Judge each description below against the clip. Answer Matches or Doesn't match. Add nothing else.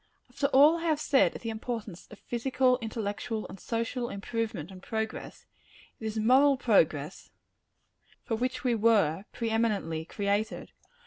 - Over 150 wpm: Doesn't match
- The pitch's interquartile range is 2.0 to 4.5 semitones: Matches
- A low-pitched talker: Doesn't match